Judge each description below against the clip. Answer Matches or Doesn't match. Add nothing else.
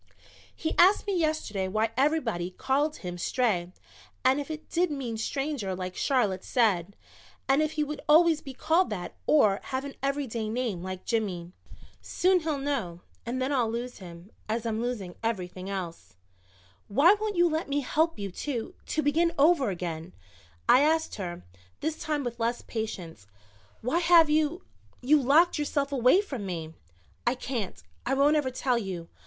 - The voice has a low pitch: Doesn't match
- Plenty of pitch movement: Matches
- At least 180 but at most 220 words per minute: Doesn't match